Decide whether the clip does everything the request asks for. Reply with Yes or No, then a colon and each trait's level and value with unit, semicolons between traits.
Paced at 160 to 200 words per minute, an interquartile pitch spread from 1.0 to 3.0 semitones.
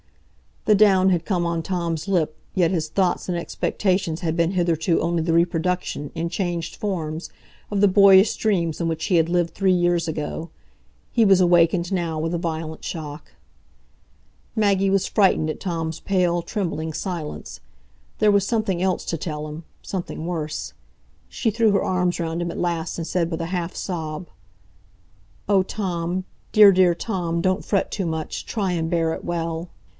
Yes: average, 170 wpm; narrow, 2.5 semitones